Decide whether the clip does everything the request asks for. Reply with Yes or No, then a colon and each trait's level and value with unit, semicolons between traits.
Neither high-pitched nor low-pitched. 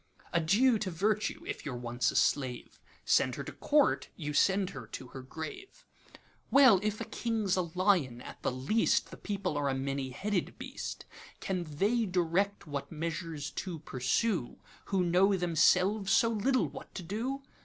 Yes: medium, 180 Hz